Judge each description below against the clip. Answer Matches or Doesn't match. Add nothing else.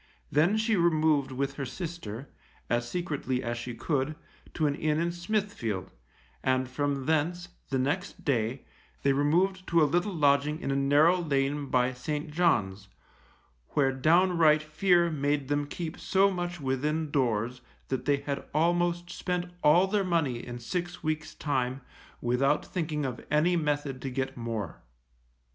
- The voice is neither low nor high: Matches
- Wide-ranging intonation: Doesn't match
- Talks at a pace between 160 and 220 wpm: Doesn't match